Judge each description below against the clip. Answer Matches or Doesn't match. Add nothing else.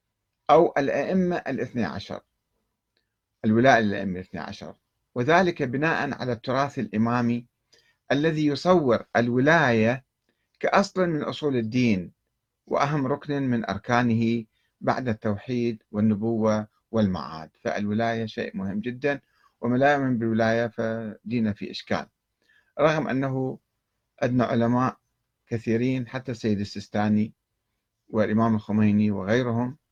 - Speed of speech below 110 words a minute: Matches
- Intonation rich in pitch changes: Doesn't match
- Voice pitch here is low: Matches